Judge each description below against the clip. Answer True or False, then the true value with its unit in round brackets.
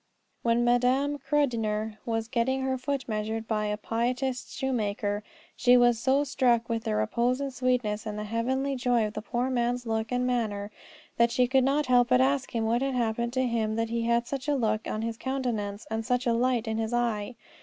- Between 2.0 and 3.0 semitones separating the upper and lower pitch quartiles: True (2.5 semitones)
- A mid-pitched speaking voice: False (240 Hz)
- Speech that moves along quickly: True (210 wpm)